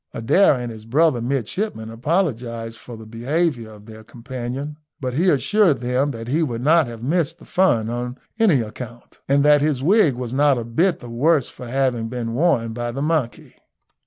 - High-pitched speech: No, low, 125 Hz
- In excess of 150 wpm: Yes, average, 190 wpm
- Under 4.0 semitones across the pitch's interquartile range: No, average, 4.5 semitones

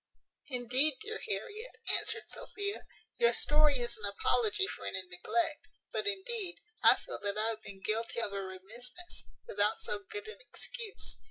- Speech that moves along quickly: No, average, 160 wpm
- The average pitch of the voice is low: No, very high, 295 Hz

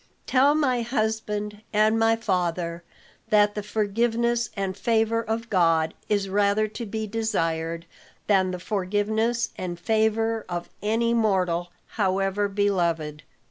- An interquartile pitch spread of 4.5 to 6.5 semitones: No, average, 3.3 semitones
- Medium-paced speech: No, slow, 125 wpm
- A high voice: Yes, high, 210 Hz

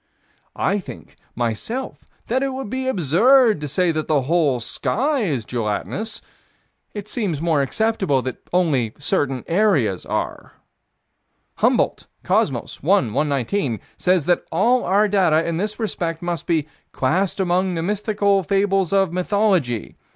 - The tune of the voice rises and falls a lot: Yes, wide, 6.1 semitones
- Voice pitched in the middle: Yes, medium, 180 Hz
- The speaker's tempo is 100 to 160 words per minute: Yes, slow, 135 wpm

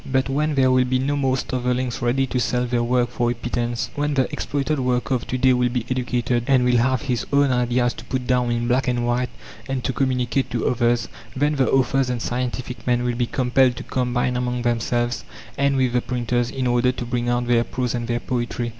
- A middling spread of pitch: No, narrow, 1.3 semitones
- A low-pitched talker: Yes, low, 125 Hz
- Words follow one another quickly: Yes, fast, 225 wpm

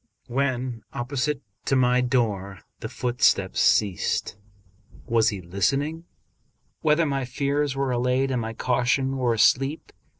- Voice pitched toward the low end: Yes, low, 125 Hz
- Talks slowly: Yes, slow, 125 wpm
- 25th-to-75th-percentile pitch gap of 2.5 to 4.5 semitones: Yes, average, 2.8 semitones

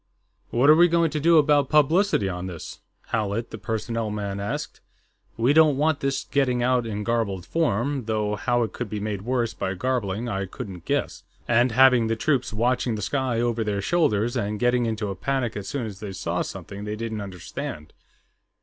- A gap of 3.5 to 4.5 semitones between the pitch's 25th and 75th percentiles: Yes, average, 4.1 semitones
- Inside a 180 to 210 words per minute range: Yes, average, 195 wpm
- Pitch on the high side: No, low, 115 Hz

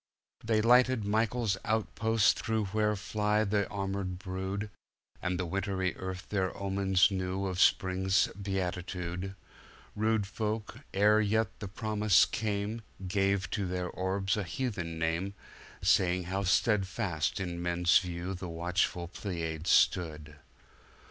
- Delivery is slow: Yes, slow, 115 wpm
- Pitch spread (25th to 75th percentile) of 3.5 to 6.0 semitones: No, average, 2.7 semitones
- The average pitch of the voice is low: Yes, very low, 95 Hz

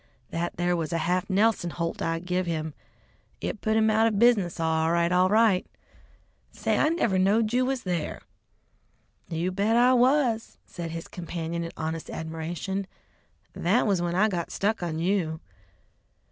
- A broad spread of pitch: No, average, 4.6 semitones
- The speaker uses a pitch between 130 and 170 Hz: No, medium, 180 Hz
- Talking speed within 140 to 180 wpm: Yes, average, 165 wpm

